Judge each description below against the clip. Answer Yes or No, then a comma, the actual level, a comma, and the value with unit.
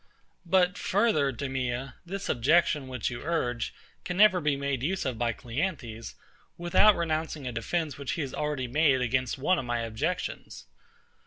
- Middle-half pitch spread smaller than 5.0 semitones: No, average, 5.3 semitones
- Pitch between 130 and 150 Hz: Yes, medium, 140 Hz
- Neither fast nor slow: Yes, average, 160 wpm